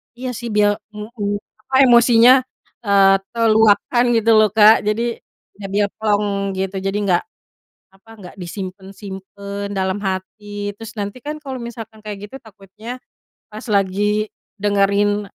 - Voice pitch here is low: No, high, 205 Hz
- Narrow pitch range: Yes, narrow, 2.1 semitones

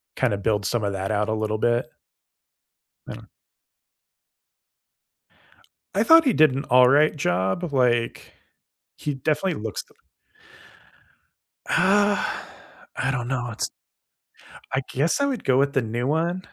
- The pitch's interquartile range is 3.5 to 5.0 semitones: No, wide, 5.6 semitones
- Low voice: Yes, low, 130 Hz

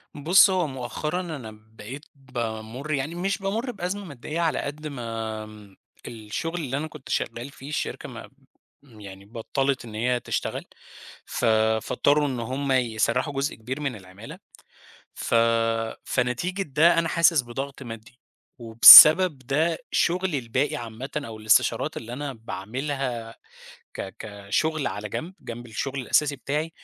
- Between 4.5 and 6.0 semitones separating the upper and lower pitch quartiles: Yes, average, 5.1 semitones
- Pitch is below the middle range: Yes, low, 130 Hz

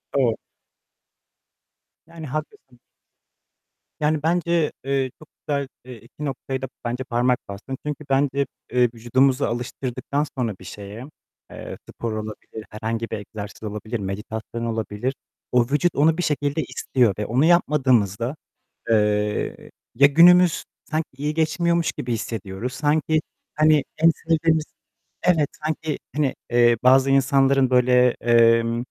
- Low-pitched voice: Yes, low, 130 Hz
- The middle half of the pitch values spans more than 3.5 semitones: Yes, average, 4.5 semitones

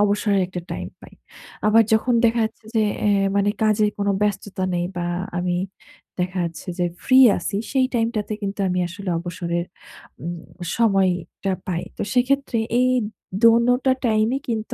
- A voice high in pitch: Yes, high, 205 Hz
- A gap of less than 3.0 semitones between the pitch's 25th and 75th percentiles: No, average, 4.1 semitones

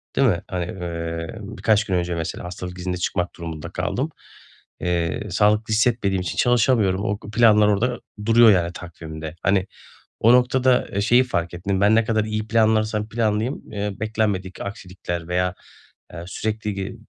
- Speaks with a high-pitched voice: No, low, 100 Hz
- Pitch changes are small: No, average, 3.7 semitones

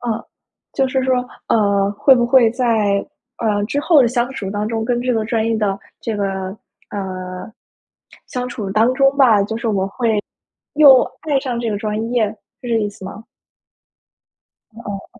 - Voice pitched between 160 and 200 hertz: No, high, 225 Hz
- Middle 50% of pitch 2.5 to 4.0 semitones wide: Yes, average, 3.3 semitones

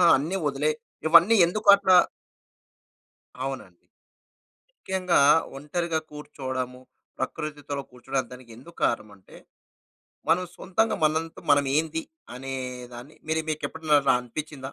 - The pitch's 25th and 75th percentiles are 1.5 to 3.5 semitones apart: No, average, 4.0 semitones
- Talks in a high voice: No, medium, 150 Hz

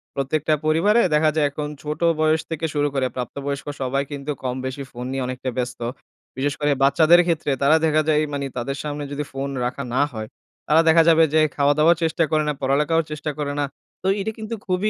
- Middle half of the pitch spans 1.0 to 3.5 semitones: Yes, narrow, 2.4 semitones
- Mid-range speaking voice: Yes, medium, 150 Hz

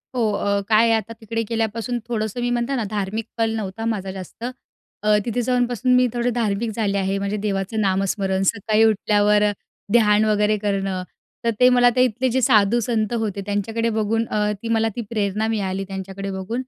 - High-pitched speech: Yes, high, 215 Hz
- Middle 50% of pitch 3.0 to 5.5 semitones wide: No, narrow, 2.6 semitones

